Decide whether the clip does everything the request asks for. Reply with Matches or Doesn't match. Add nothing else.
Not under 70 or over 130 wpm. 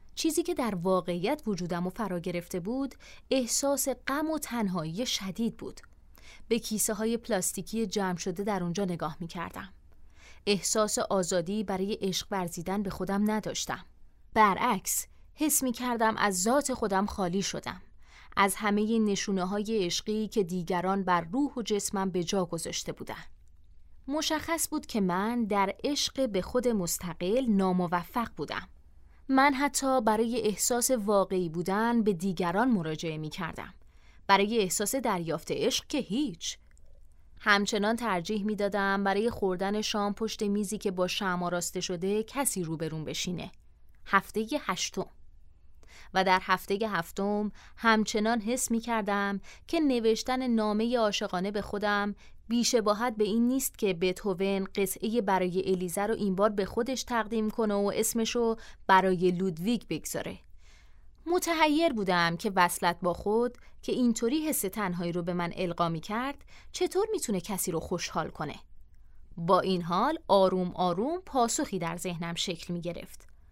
Doesn't match